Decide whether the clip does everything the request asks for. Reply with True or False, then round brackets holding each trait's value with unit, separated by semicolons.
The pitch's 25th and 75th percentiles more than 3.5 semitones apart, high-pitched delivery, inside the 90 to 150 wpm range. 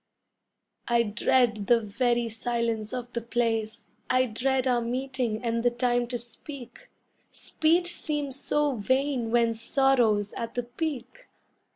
False (2.4 semitones; 240 Hz; 135 wpm)